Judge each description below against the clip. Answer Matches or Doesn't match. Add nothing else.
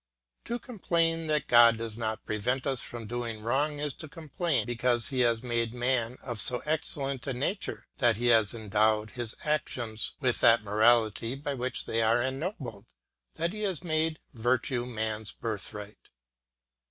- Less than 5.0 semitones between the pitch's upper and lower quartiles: Matches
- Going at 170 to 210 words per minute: Doesn't match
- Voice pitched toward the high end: Doesn't match